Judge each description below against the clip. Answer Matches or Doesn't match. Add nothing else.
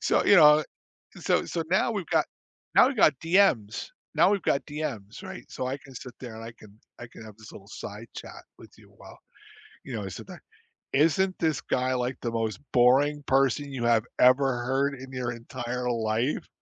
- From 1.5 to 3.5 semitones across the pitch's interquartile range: Doesn't match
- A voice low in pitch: Matches